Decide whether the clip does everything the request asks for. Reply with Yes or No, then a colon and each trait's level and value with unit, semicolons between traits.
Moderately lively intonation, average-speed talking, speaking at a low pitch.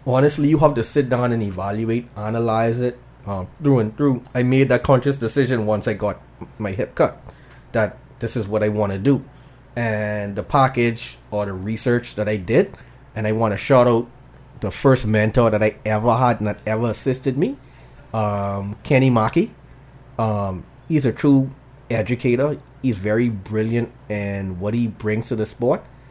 Yes: average, 3.4 semitones; average, 180 wpm; low, 115 Hz